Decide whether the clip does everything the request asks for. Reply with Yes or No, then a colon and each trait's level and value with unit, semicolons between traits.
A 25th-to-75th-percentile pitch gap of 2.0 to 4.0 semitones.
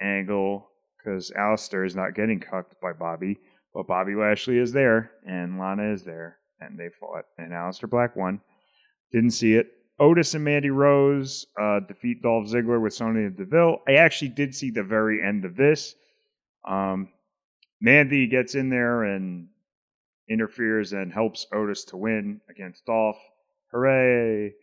No: average, 5.0 semitones